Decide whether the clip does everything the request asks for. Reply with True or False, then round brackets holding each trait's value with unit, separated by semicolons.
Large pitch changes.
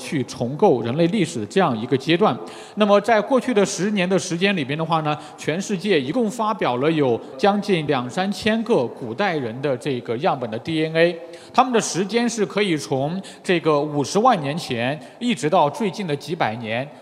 True (5.9 semitones)